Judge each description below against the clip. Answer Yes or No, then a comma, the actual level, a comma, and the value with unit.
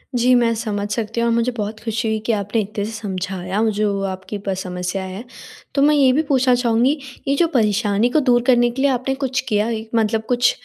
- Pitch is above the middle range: Yes, high, 225 Hz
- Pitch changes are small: No, average, 3.4 semitones